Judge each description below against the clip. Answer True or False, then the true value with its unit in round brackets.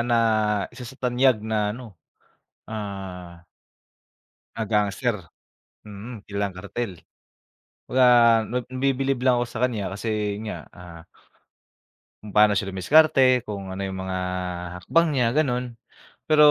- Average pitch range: True (3.9 semitones)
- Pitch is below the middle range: True (110 Hz)